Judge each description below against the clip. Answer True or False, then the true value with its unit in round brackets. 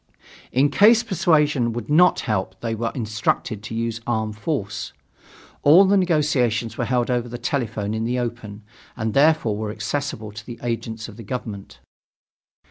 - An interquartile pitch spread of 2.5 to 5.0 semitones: True (4.5 semitones)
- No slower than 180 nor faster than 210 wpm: False (160 wpm)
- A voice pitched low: True (115 Hz)